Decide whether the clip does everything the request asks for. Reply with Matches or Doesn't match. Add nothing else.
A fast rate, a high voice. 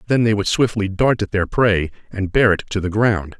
Doesn't match